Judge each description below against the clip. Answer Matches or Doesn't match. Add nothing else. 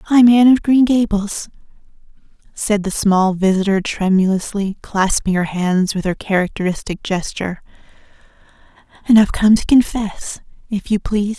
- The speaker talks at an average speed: Doesn't match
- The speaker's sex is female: Matches